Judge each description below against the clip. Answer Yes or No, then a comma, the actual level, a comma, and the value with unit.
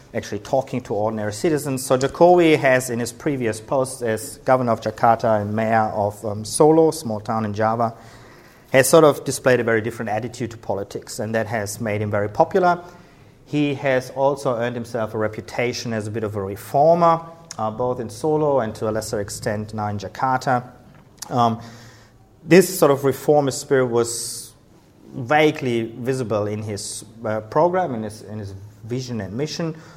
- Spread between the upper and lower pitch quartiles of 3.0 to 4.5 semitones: Yes, average, 4.0 semitones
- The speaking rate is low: No, average, 175 wpm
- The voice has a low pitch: Yes, low, 120 Hz